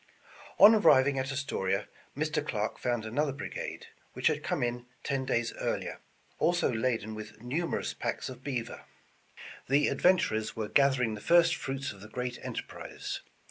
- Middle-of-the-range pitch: No, low, 130 Hz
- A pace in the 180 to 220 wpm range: No, average, 150 wpm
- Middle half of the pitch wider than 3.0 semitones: Yes, average, 4.2 semitones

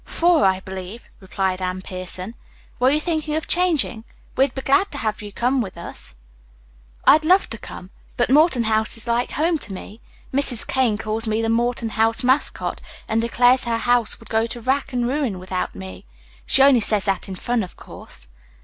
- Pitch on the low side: No, high, 230 Hz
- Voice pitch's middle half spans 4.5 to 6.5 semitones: Yes, average, 4.9 semitones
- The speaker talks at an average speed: Yes, average, 190 wpm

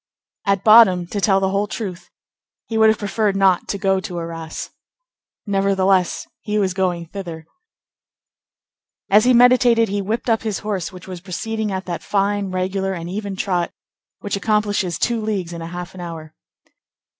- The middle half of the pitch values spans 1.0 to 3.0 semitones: Yes, average, 2.7 semitones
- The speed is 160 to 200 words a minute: Yes, average, 165 wpm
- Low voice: No, high, 195 Hz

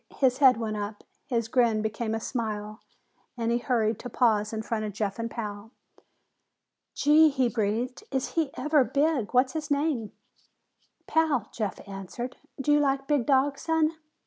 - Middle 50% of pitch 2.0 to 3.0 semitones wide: No, average, 4.3 semitones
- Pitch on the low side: No, high, 240 Hz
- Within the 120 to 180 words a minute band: Yes, average, 165 wpm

